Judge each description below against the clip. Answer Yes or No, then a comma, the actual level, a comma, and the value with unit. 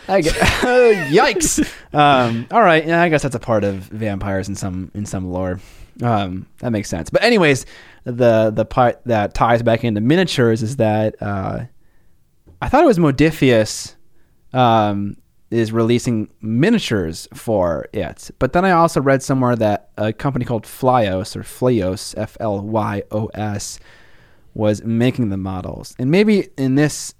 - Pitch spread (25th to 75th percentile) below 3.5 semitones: No, average, 3.9 semitones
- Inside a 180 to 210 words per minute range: No, average, 150 wpm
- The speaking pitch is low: Yes, low, 110 Hz